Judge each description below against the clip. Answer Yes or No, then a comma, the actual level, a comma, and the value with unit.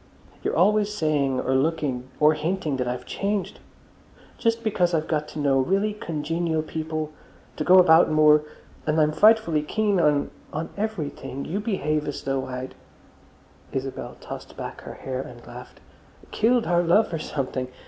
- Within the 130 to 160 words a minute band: Yes, average, 150 wpm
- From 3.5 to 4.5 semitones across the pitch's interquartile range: No, average, 5.1 semitones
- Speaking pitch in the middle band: Yes, medium, 155 Hz